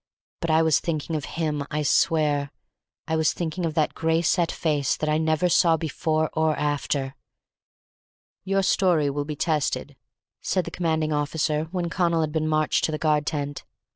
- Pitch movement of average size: No, narrow, 1.6 semitones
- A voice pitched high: No, medium, 155 Hz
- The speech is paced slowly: No, average, 175 wpm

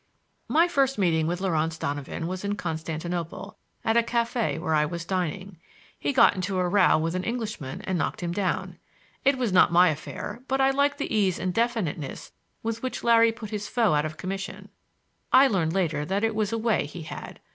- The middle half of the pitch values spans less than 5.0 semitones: No, wide, 5.5 semitones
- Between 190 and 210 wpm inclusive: Yes, average, 200 wpm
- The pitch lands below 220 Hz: Yes, high, 190 Hz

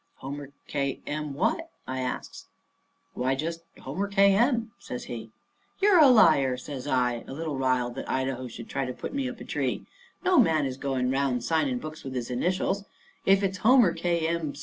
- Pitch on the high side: No, medium, 145 Hz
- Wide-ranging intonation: Yes, wide, 6.9 semitones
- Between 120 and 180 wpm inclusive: No, average, 190 wpm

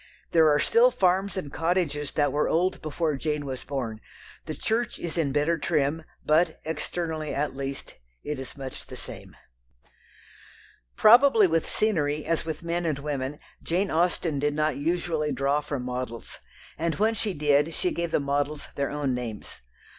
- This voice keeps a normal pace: Yes, average, 165 wpm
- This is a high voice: No, medium, 150 Hz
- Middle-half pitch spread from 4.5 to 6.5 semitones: No, average, 3.2 semitones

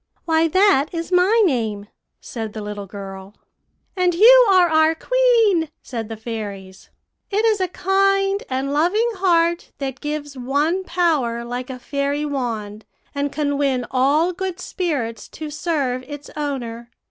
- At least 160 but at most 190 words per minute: No, average, 145 wpm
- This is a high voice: Yes, very high, 290 Hz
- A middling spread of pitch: No, wide, 6.8 semitones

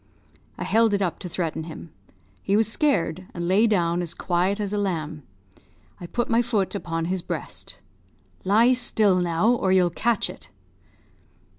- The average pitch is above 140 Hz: Yes, high, 190 Hz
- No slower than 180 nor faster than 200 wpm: No, average, 165 wpm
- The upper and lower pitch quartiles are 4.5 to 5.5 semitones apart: No, average, 4.1 semitones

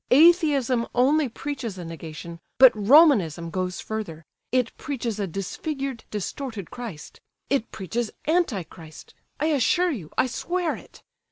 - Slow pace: Yes, slow, 120 wpm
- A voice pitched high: Yes, high, 235 Hz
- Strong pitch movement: Yes, wide, 7.4 semitones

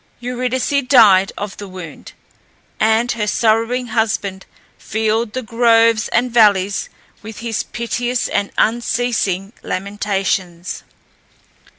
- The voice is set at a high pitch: Yes, high, 220 Hz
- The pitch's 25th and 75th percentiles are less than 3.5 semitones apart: Yes, average, 3.1 semitones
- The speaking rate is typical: No, slow, 100 wpm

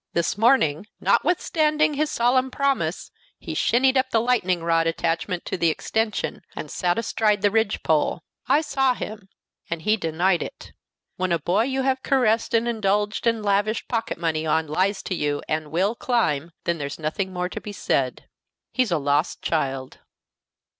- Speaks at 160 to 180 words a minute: Yes, average, 170 wpm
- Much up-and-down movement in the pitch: Yes, wide, 6.3 semitones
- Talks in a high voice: Yes, high, 200 Hz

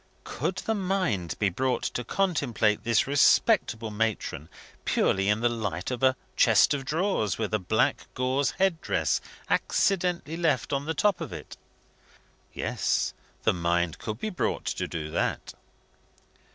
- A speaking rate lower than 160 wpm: Yes, average, 150 wpm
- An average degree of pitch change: No, wide, 8.0 semitones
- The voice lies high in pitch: No, low, 125 Hz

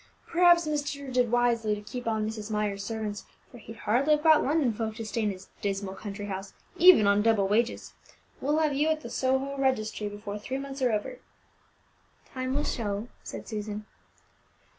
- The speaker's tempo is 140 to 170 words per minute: No, average, 185 wpm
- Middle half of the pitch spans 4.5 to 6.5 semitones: Yes, average, 4.8 semitones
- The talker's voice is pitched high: Yes, high, 225 Hz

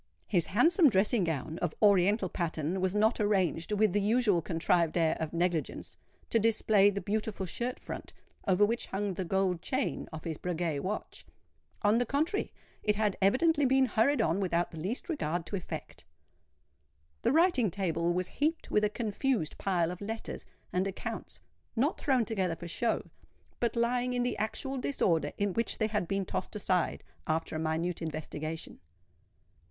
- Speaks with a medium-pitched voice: No, high, 200 Hz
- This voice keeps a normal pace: Yes, average, 165 wpm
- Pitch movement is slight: No, average, 5.1 semitones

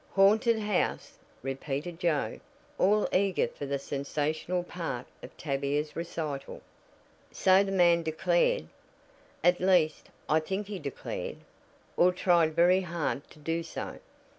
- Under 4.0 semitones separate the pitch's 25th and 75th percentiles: Yes, average, 3.6 semitones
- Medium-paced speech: No, slow, 125 wpm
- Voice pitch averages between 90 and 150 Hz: No, medium, 170 Hz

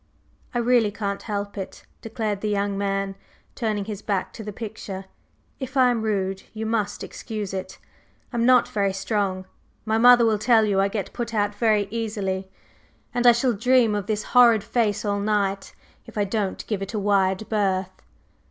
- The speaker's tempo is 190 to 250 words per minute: No, average, 180 wpm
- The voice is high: Yes, high, 210 Hz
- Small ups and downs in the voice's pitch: Yes, narrow, 2.3 semitones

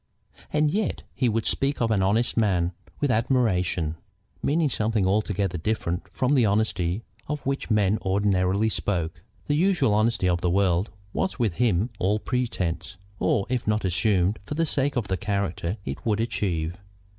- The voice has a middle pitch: No, low, 105 Hz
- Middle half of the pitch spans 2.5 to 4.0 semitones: No, average, 4.7 semitones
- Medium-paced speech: Yes, average, 165 wpm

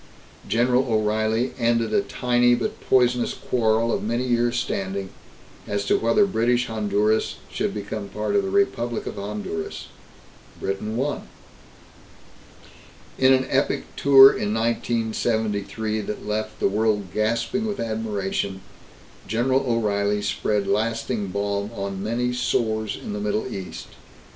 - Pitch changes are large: No, average, 2.7 semitones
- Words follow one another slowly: Yes, slow, 130 wpm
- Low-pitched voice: Yes, low, 110 Hz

